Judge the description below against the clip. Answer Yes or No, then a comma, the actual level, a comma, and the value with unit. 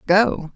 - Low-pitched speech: No, high, 190 Hz